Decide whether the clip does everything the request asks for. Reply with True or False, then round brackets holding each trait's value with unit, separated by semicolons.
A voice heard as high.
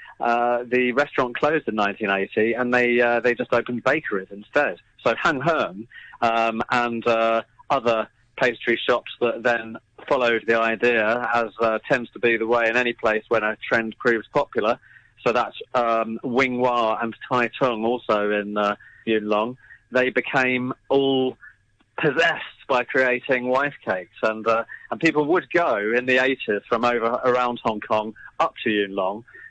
False (120 Hz)